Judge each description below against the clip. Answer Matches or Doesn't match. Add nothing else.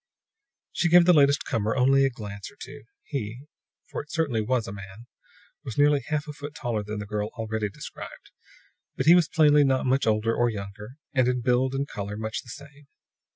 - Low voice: Matches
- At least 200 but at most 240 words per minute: Matches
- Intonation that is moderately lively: Matches